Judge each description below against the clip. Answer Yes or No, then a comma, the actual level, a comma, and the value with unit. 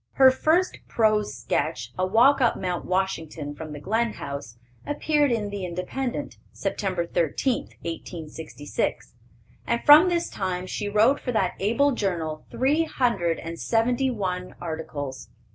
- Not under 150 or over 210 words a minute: No, average, 140 wpm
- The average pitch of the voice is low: No, high, 195 Hz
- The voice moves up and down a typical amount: No, wide, 6.9 semitones